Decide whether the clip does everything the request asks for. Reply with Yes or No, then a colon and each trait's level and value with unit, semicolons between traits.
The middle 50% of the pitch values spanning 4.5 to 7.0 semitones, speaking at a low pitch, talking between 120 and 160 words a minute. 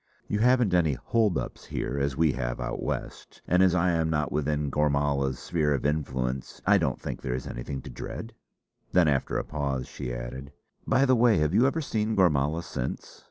No: average, 5.3 semitones; very low, 75 Hz; average, 200 wpm